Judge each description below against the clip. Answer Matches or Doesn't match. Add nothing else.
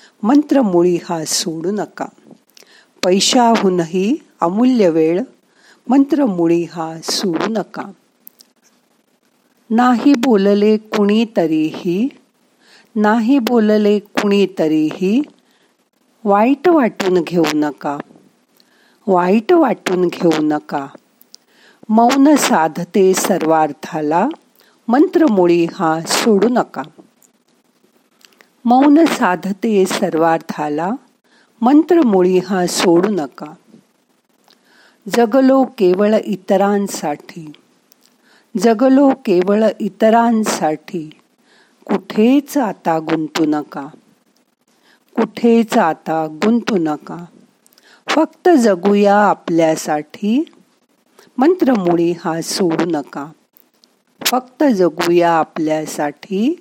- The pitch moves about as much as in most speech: Doesn't match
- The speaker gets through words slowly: Matches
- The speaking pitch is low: Doesn't match